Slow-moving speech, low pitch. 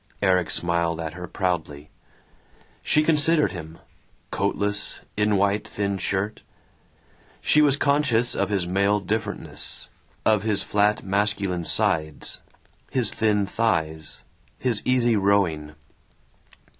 Yes: slow, 110 wpm; low, 100 Hz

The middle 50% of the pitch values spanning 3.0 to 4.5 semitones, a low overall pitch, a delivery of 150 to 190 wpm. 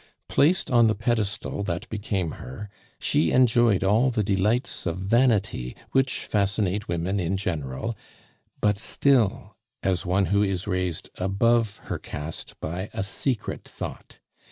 No: average, 3.7 semitones; low, 100 Hz; slow, 135 wpm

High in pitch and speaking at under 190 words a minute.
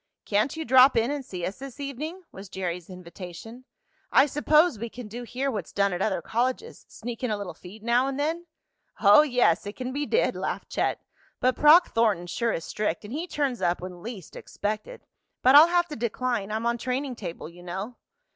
No: high, 235 Hz; fast, 205 wpm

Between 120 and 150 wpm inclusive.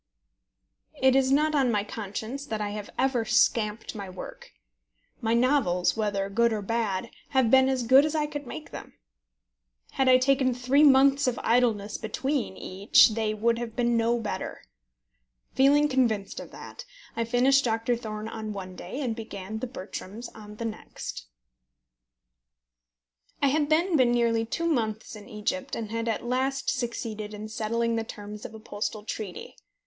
No: average, 165 wpm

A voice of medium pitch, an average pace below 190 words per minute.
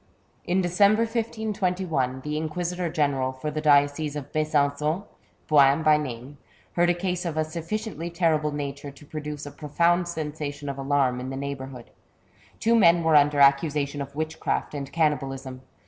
Yes: medium, 150 Hz; average, 155 wpm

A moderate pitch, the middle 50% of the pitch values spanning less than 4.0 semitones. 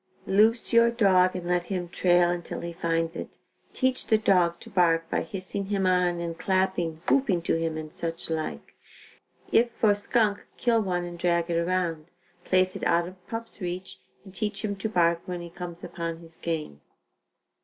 Yes: medium, 180 Hz; average, 2.7 semitones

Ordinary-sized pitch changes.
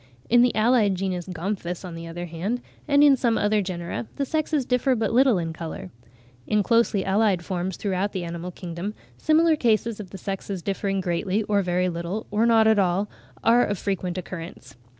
Yes: average, 4.2 semitones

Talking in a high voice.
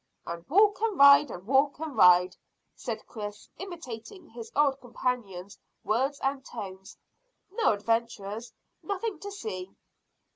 Yes: very high, 250 Hz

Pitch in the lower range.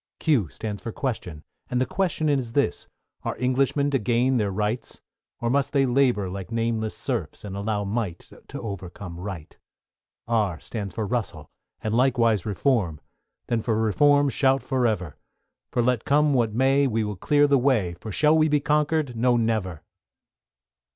Yes: low, 115 Hz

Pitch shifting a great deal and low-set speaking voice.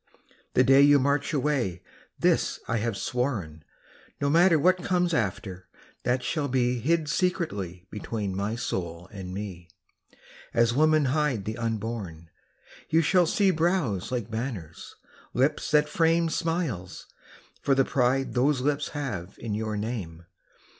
Yes: wide, 6.9 semitones; low, 125 Hz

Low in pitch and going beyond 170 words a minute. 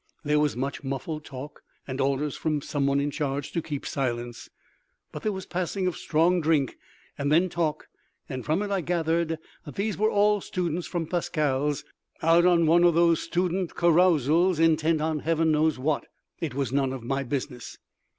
No: medium, 155 Hz; average, 180 wpm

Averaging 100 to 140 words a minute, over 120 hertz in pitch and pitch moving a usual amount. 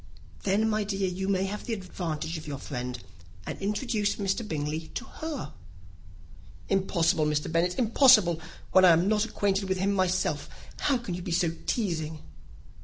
No: average, 165 wpm; high, 190 Hz; average, 4.1 semitones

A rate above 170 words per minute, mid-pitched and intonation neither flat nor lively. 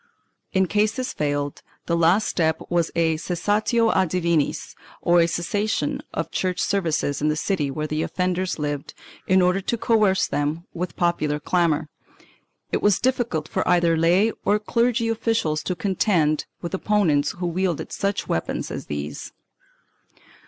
No: average, 150 wpm; medium, 175 Hz; average, 4.3 semitones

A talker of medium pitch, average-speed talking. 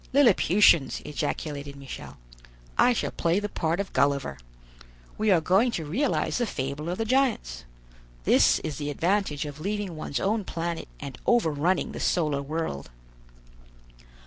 Yes: medium, 165 Hz; average, 145 wpm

